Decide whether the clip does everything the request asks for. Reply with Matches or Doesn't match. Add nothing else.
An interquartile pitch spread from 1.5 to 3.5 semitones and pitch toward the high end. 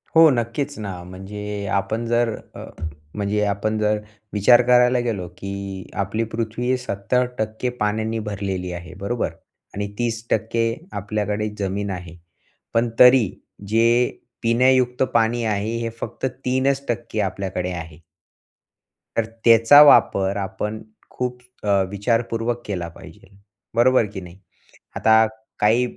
Doesn't match